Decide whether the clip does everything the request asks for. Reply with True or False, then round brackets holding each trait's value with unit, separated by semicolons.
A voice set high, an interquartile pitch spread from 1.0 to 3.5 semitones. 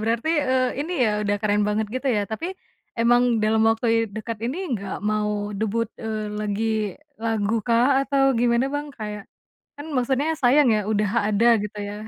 True (225 Hz; 2.9 semitones)